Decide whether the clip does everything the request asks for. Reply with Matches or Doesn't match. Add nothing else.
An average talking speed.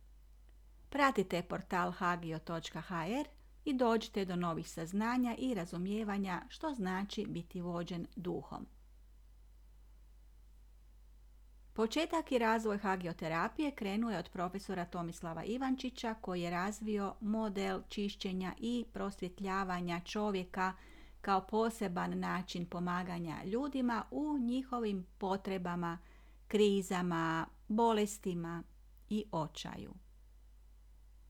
Doesn't match